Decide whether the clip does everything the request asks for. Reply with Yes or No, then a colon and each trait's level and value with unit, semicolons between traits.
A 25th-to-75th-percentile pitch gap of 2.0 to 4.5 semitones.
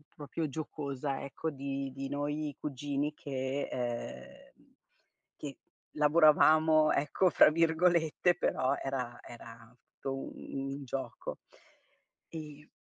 Yes: narrow, 2.4 semitones